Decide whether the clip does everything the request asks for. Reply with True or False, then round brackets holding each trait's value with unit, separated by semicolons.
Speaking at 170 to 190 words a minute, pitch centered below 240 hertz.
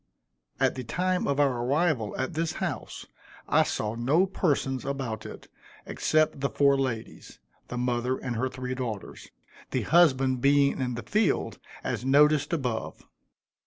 False (150 wpm; 135 Hz)